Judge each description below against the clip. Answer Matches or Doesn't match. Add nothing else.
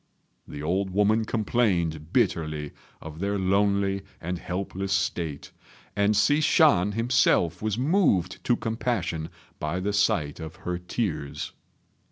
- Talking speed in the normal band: Doesn't match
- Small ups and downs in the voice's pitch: Doesn't match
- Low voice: Matches